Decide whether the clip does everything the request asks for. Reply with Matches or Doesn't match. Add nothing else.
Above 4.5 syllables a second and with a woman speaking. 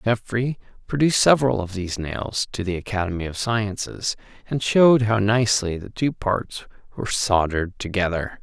Doesn't match